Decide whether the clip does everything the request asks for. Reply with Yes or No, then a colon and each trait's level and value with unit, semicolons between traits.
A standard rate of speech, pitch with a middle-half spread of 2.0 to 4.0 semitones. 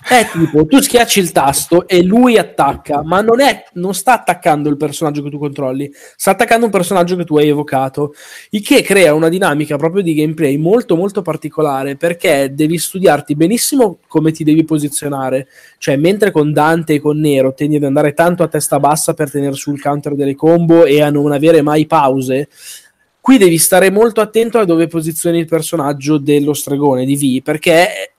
No: fast, 185 wpm; average, 3.4 semitones